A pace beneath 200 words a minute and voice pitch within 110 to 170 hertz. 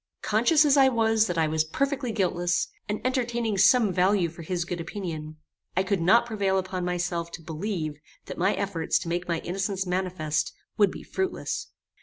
No: average, 180 wpm; medium, 185 Hz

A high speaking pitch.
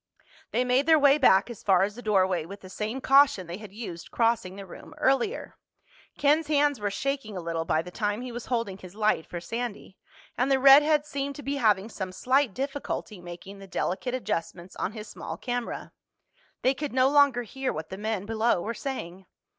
Yes: high, 225 Hz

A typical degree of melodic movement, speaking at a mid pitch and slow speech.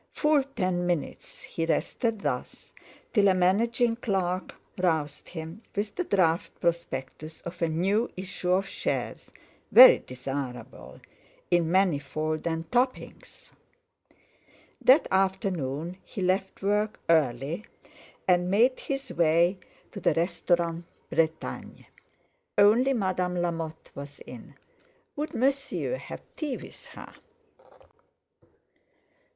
Yes: average, 4.3 semitones; medium, 180 Hz; slow, 110 wpm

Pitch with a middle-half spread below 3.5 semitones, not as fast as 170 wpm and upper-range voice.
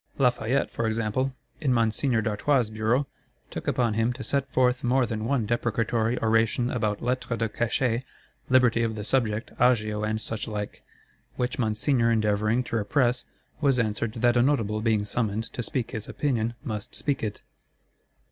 No: narrow, 2.5 semitones; average, 155 wpm; low, 115 Hz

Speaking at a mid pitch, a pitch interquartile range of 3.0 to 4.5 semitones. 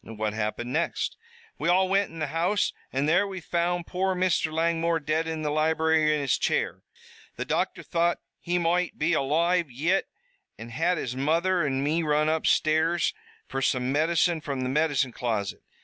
Yes: medium, 160 Hz; average, 3.4 semitones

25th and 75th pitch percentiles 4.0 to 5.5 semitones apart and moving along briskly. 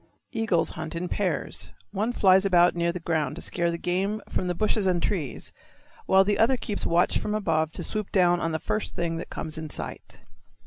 No: average, 3.4 semitones; fast, 210 wpm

